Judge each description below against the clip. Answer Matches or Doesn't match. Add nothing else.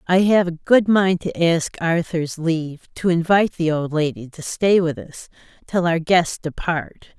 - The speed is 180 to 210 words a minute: Matches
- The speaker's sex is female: Matches